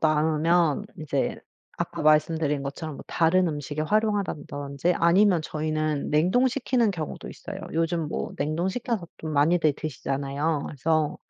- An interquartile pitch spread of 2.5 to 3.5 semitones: Yes, average, 2.8 semitones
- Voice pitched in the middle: Yes, medium, 155 Hz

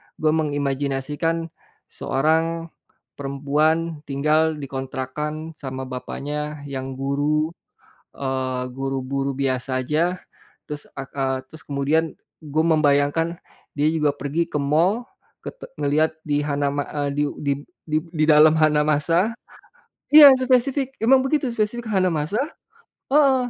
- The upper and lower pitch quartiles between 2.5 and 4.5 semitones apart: Yes, average, 2.8 semitones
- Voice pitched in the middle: Yes, medium, 150 Hz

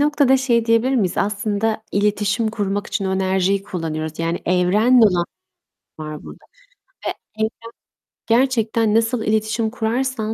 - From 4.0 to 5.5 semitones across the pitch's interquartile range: No, average, 3.2 semitones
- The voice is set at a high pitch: Yes, high, 215 Hz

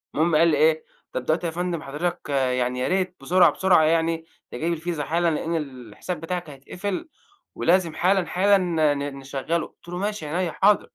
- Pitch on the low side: No, medium, 165 Hz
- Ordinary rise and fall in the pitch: Yes, average, 3.3 semitones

